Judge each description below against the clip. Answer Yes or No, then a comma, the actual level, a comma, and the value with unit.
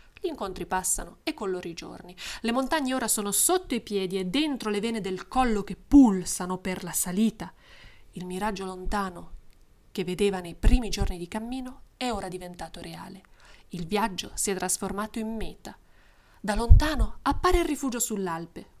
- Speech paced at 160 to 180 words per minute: Yes, average, 165 wpm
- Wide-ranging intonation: No, average, 4.1 semitones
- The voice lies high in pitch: Yes, high, 205 Hz